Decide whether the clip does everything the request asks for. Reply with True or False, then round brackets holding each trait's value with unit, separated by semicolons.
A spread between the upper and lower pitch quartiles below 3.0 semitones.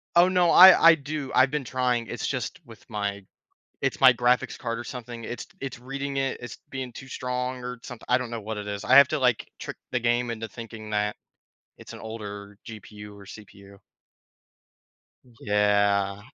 False (3.6 semitones)